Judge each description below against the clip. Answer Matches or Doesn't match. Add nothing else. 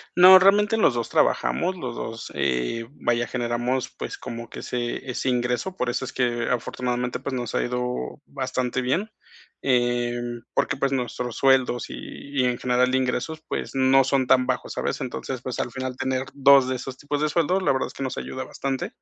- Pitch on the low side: Matches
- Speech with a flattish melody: Matches